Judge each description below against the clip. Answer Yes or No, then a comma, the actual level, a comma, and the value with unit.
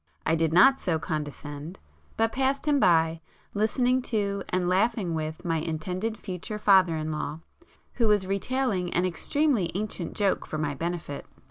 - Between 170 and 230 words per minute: No, average, 150 wpm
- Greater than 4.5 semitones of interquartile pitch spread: Yes, average, 5.1 semitones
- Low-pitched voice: No, medium, 185 Hz